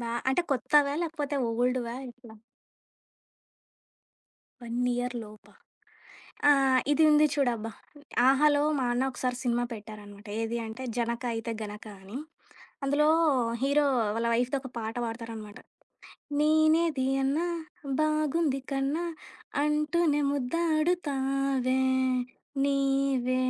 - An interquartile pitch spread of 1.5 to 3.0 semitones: No, average, 3.9 semitones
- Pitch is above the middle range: Yes, very high, 265 Hz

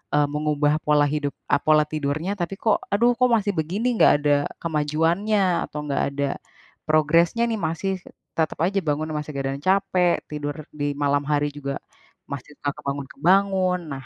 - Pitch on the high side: No, medium, 155 Hz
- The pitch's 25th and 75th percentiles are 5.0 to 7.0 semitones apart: No, average, 4.2 semitones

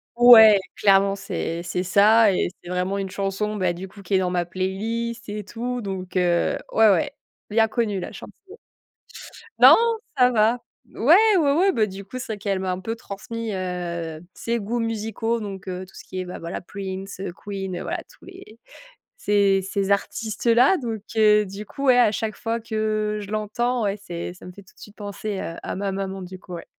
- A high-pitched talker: Yes, high, 205 Hz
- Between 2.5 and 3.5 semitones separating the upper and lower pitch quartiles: Yes, average, 3.0 semitones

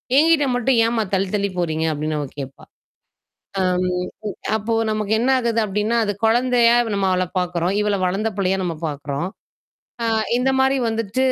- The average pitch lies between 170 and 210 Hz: Yes, high, 205 Hz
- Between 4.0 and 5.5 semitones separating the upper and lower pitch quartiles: Yes, average, 4.6 semitones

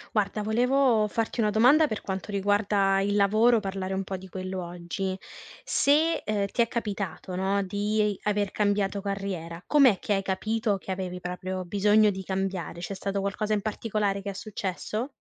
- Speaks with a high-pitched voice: Yes, high, 200 Hz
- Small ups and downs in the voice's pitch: Yes, narrow, 2.0 semitones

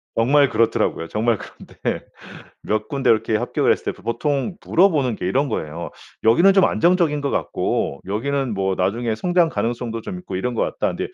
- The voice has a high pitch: No, low, 120 Hz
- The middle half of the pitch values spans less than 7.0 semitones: Yes, average, 5.2 semitones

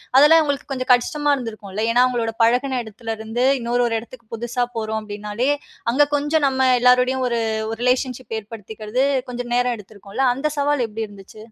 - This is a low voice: No, high, 245 Hz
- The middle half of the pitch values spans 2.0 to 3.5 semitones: Yes, average, 3.0 semitones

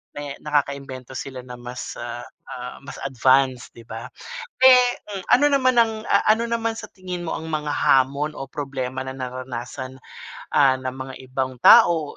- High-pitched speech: No, low, 135 Hz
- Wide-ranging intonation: No, average, 3.9 semitones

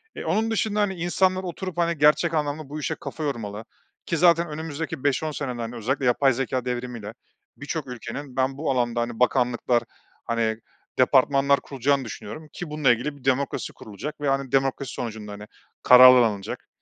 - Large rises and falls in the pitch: No, average, 4.0 semitones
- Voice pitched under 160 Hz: Yes, low, 135 Hz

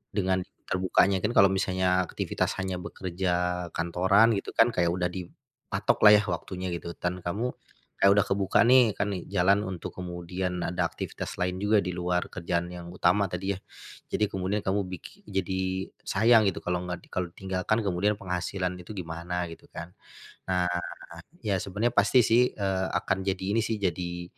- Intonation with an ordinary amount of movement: No, narrow, 2.1 semitones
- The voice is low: Yes, very low, 95 Hz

